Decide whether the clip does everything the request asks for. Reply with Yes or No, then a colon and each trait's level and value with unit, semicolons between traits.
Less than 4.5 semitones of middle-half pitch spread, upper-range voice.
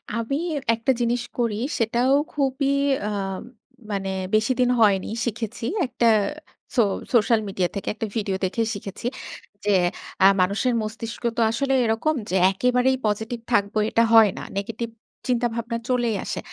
Yes: average, 2.8 semitones; high, 230 Hz